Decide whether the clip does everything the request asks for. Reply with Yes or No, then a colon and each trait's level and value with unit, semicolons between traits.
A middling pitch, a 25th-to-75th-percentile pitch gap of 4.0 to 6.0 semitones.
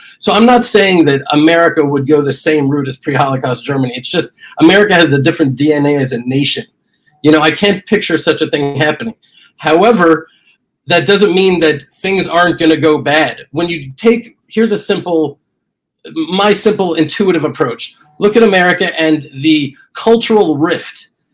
Yes: medium, 160 Hz; average, 5.1 semitones